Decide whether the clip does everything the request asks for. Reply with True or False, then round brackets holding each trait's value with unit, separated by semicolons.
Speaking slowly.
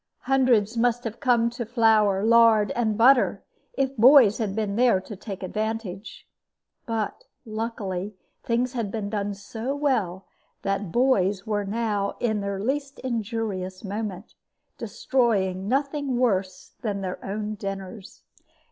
True (130 wpm)